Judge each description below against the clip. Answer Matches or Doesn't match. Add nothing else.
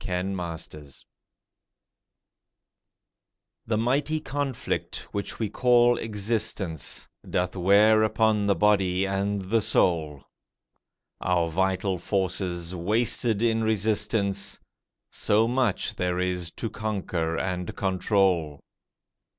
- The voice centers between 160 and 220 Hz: Doesn't match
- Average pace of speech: Doesn't match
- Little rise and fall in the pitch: Doesn't match